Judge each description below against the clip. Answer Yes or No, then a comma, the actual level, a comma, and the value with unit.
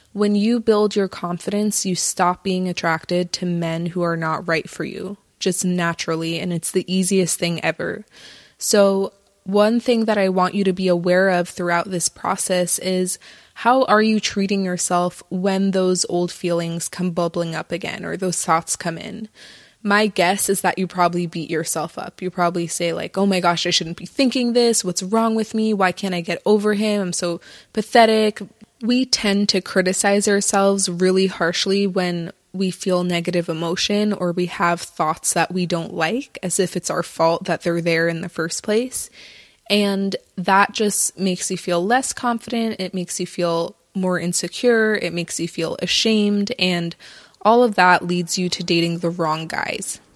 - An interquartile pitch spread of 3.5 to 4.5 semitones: No, average, 2.8 semitones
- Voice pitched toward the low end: No, medium, 185 Hz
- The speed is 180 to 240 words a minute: Yes, average, 185 wpm